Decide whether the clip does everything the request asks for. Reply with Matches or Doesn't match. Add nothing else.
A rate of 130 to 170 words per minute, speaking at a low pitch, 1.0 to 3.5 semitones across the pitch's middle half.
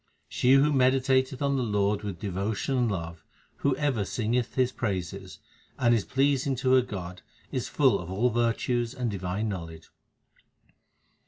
Doesn't match